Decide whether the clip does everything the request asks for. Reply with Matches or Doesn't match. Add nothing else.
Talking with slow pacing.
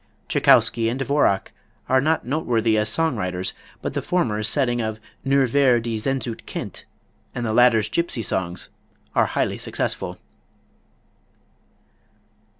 Matches